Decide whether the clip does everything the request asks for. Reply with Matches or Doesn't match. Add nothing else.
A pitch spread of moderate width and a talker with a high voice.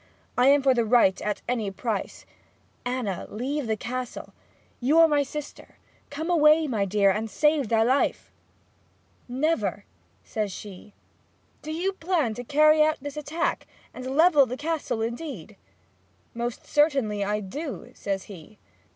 Doesn't match